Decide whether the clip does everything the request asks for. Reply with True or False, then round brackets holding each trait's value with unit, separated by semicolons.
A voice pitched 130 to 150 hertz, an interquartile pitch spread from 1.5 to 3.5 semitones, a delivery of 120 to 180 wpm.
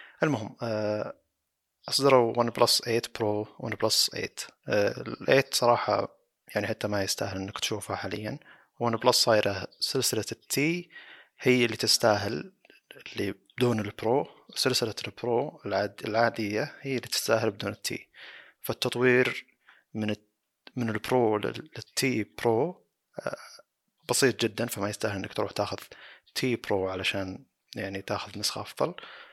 False (110 Hz; 3.0 semitones; 125 wpm)